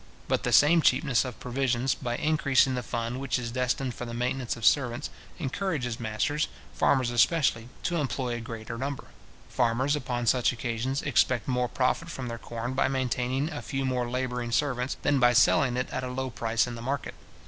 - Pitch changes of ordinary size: No, narrow, 2.2 semitones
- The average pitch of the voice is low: Yes, low, 125 Hz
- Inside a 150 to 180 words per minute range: No, average, 190 wpm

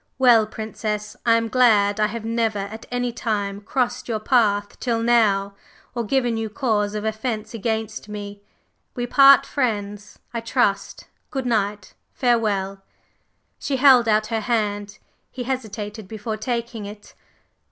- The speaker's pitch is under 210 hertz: No, high, 220 Hz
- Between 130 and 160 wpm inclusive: Yes, average, 140 wpm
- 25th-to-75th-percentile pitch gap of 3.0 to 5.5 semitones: No, narrow, 2.6 semitones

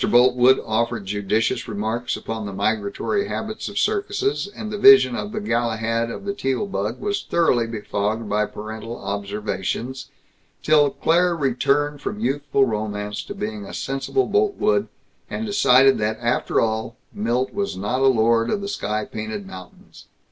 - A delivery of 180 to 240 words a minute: No, average, 155 wpm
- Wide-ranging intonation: Yes, wide, 7.0 semitones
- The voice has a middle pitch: No, low, 120 Hz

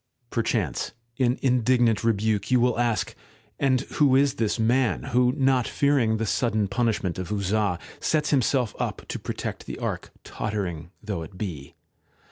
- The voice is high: No, low, 115 Hz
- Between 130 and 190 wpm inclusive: Yes, average, 150 wpm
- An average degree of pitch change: Yes, average, 3.7 semitones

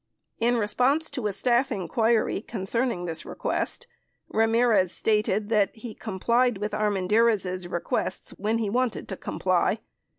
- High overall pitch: Yes, high, 220 Hz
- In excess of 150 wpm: No, average, 140 wpm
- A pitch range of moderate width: Yes, average, 3.2 semitones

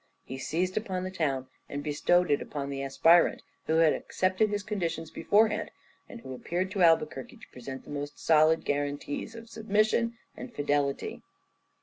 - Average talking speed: Yes, average, 160 wpm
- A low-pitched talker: No, medium, 165 Hz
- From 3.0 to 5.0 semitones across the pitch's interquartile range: No, wide, 5.6 semitones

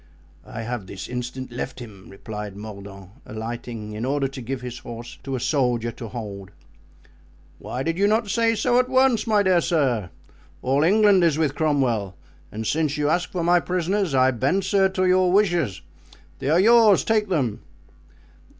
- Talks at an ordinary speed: Yes, average, 175 wpm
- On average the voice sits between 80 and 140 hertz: Yes, low, 135 Hz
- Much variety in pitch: Yes, wide, 8.1 semitones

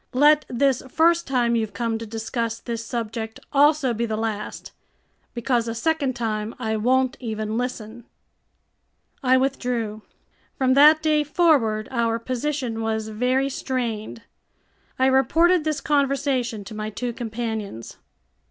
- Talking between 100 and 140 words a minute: Yes, slow, 135 wpm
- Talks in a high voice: Yes, high, 240 Hz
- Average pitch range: Yes, average, 3.4 semitones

